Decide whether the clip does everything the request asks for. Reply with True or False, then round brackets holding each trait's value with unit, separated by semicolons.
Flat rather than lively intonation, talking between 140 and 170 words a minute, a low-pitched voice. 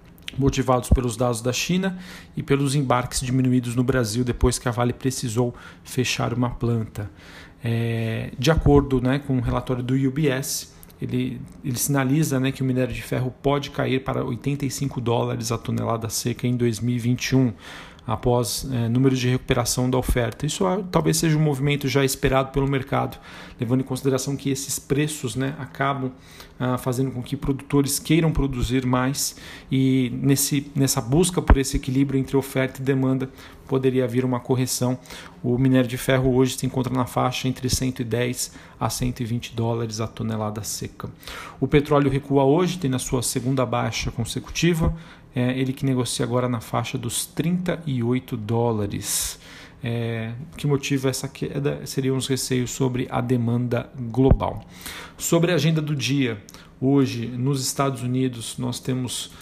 True (2.0 semitones; 160 wpm; 130 Hz)